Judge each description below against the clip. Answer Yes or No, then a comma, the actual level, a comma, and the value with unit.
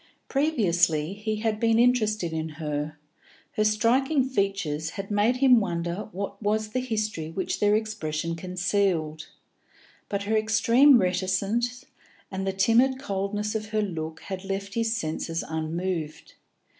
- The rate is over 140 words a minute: No, slow, 135 wpm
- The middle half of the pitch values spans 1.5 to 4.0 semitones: No, average, 4.5 semitones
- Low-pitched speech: No, high, 200 Hz